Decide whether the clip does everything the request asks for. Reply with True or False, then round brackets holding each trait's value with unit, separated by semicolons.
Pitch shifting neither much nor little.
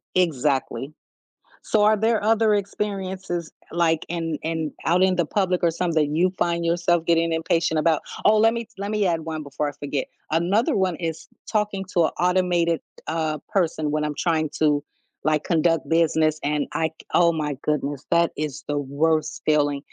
True (3.1 semitones)